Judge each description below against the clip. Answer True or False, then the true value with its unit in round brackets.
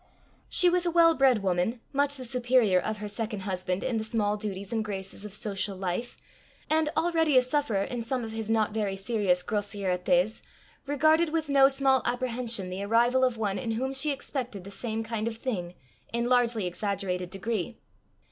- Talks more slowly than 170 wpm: False (185 wpm)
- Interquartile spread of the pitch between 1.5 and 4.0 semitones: False (4.6 semitones)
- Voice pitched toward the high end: True (225 Hz)